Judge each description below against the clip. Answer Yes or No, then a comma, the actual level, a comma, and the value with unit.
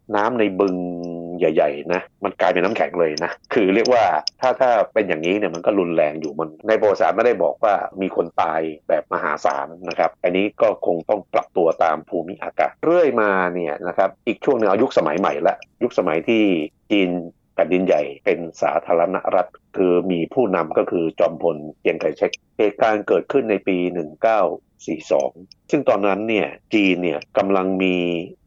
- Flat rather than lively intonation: Yes, narrow, 2.3 semitones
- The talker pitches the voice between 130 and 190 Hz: No, very low, 90 Hz